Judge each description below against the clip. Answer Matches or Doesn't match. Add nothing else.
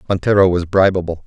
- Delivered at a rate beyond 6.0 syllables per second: Matches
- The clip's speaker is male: Matches